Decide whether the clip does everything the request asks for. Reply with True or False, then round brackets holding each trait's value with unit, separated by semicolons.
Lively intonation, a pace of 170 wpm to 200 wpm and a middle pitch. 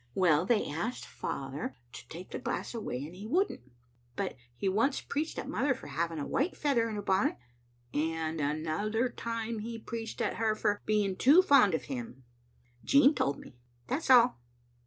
False (7.0 semitones; 180 wpm; 215 Hz)